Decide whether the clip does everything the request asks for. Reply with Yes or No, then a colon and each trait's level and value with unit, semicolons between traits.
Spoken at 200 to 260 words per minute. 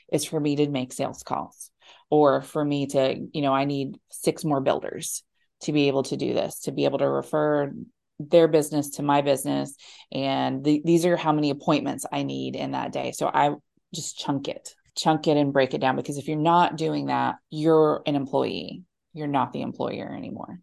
Yes: fast, 205 wpm